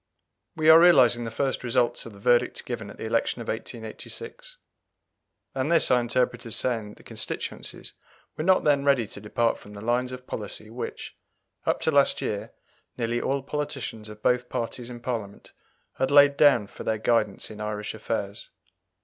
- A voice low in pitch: Yes, low, 120 Hz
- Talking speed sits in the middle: Yes, average, 180 wpm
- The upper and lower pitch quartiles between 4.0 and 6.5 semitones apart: No, average, 3.6 semitones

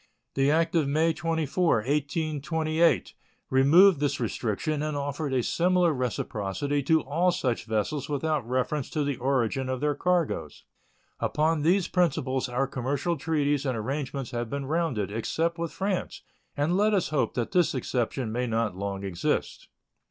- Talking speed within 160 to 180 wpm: No, average, 150 wpm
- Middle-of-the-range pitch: Yes, medium, 145 Hz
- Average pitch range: Yes, average, 4.3 semitones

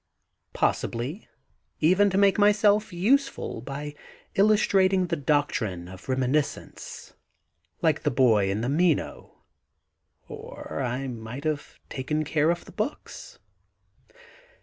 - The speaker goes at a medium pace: No, slow, 115 wpm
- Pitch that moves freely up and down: Yes, wide, 7.3 semitones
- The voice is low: No, medium, 150 Hz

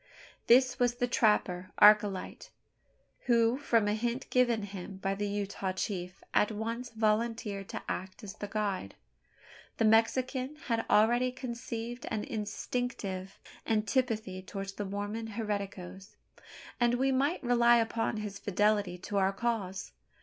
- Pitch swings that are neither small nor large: Yes, average, 3.2 semitones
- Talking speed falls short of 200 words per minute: Yes, slow, 135 wpm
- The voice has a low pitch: No, high, 215 Hz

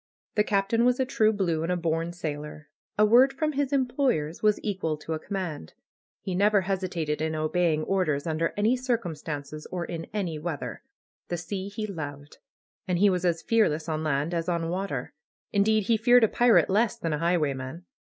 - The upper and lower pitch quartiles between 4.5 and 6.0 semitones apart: Yes, average, 5.2 semitones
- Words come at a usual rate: Yes, average, 185 wpm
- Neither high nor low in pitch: Yes, medium, 180 Hz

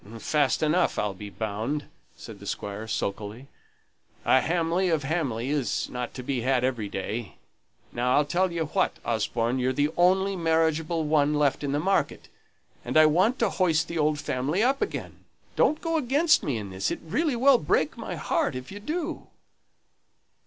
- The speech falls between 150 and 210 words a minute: Yes, average, 175 wpm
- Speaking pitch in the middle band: Yes, medium, 150 Hz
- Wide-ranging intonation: Yes, wide, 6.6 semitones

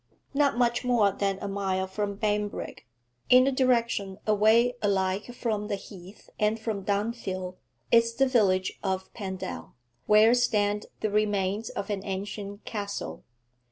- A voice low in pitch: No, high, 205 Hz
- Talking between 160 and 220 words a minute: No, average, 140 wpm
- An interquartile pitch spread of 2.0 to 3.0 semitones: Yes, average, 2.7 semitones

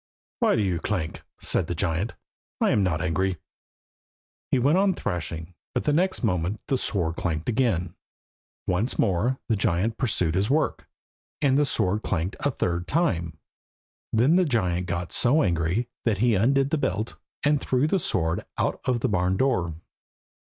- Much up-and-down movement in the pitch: Yes, wide, 7.0 semitones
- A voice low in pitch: Yes, low, 100 Hz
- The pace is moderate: Yes, average, 165 wpm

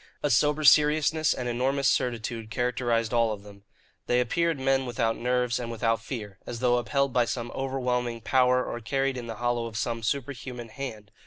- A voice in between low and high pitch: No, low, 125 Hz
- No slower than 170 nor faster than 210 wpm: Yes, average, 180 wpm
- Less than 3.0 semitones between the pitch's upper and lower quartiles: Yes, narrow, 2.5 semitones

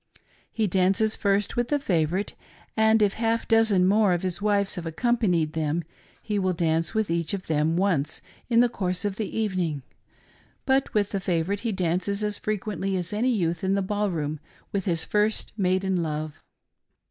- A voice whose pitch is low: No, high, 195 Hz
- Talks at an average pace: Yes, average, 180 wpm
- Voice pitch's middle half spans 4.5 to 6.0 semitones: No, average, 3.8 semitones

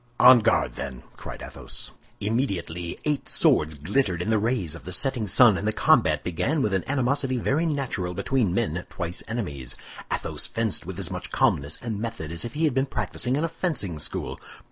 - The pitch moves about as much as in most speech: No, wide, 7.2 semitones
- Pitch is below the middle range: Yes, low, 110 Hz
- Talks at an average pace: Yes, average, 190 wpm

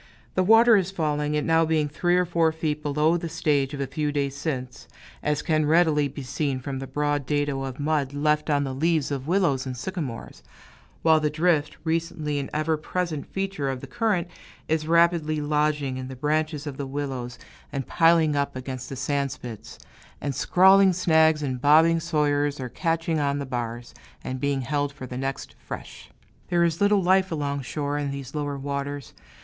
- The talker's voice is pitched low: No, medium, 150 Hz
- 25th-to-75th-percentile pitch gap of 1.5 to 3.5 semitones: Yes, average, 2.8 semitones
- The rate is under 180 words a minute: No, average, 190 wpm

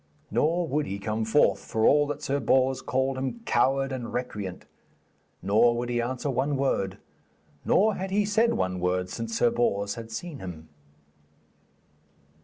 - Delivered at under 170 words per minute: Yes, average, 160 wpm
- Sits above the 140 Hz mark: No, low, 125 Hz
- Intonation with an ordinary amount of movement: Yes, average, 5.0 semitones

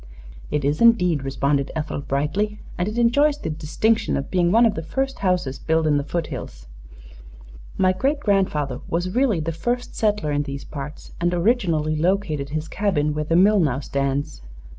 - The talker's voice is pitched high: No, medium, 165 Hz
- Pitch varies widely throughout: Yes, wide, 6.1 semitones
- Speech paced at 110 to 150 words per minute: No, average, 175 wpm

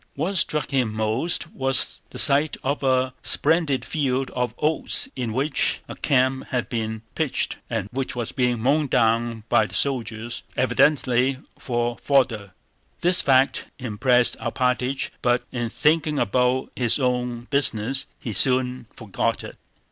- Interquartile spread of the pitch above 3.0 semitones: No, narrow, 2.5 semitones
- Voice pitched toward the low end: Yes, low, 130 Hz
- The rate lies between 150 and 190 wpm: No, average, 140 wpm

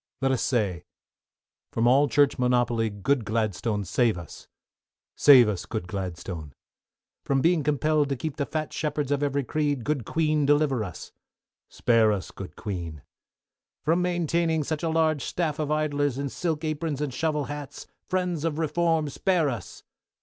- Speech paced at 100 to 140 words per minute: No, average, 155 wpm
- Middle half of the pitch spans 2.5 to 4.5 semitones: No, average, 5.2 semitones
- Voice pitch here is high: No, medium, 145 Hz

